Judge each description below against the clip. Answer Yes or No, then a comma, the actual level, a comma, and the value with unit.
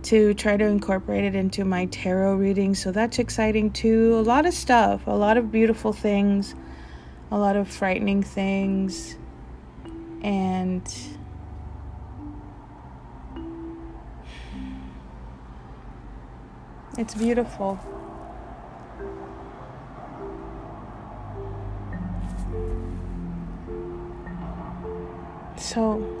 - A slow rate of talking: Yes, slow, 70 wpm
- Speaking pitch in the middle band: No, low, 100 Hz